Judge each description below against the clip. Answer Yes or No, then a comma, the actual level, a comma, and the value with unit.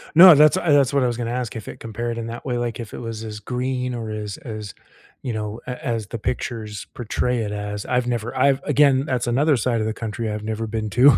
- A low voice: Yes, low, 120 Hz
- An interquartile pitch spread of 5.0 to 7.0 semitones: No, average, 2.7 semitones